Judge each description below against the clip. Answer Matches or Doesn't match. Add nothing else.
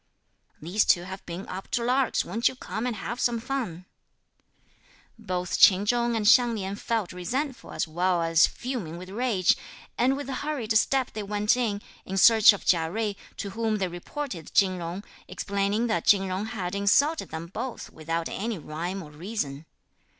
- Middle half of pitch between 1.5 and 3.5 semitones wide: Doesn't match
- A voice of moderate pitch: Doesn't match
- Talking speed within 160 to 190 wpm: Matches